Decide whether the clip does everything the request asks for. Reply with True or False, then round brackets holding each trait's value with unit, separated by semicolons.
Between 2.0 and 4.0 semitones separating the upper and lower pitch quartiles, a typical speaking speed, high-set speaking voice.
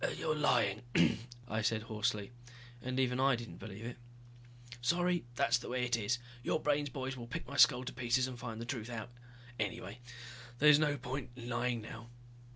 False (2.6 semitones; 180 wpm; 125 Hz)